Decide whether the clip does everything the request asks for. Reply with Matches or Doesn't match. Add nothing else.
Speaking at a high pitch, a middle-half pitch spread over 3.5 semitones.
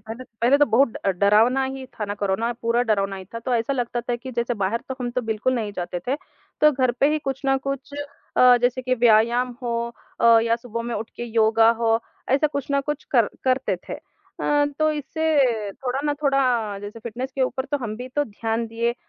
Doesn't match